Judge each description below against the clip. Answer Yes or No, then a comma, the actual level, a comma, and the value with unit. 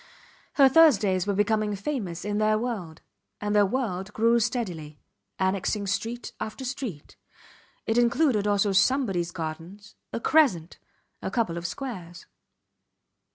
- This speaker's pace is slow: Yes, slow, 125 wpm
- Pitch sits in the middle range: No, high, 210 Hz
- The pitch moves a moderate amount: Yes, average, 4.4 semitones